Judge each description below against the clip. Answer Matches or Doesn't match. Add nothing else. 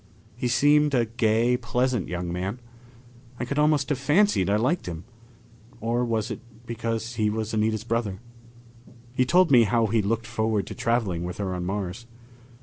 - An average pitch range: Matches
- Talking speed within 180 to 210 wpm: Doesn't match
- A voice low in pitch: Matches